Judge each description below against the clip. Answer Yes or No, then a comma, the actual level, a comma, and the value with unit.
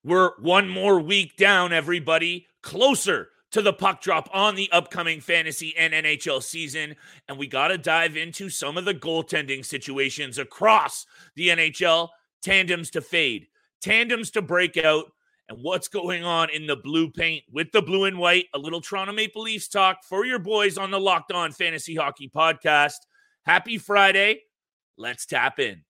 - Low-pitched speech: No, medium, 175 Hz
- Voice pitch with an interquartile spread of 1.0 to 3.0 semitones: No, average, 3.5 semitones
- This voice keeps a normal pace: Yes, average, 170 wpm